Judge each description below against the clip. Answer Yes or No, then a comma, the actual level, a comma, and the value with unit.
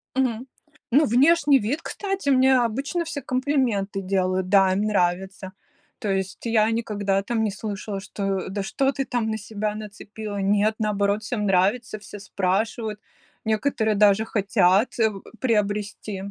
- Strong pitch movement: No, average, 3.3 semitones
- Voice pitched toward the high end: Yes, high, 210 Hz